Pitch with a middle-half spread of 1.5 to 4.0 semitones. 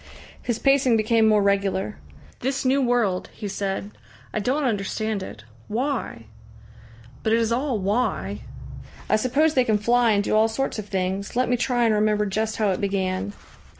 Yes: average, 3.6 semitones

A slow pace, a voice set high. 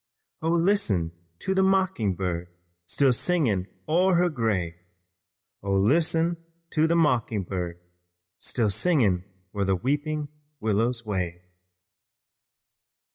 No: slow, 110 wpm; low, 115 Hz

